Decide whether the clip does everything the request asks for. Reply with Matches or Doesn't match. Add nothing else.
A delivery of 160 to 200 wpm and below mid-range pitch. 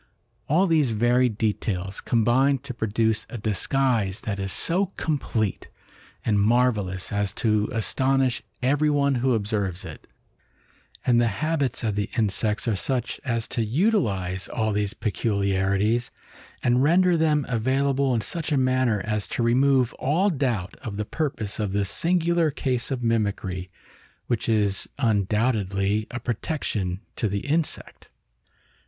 Doesn't match